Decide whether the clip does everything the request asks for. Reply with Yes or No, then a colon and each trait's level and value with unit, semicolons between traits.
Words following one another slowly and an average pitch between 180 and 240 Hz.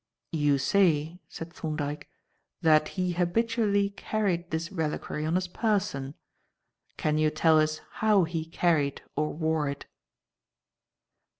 No: slow, 120 wpm; medium, 160 Hz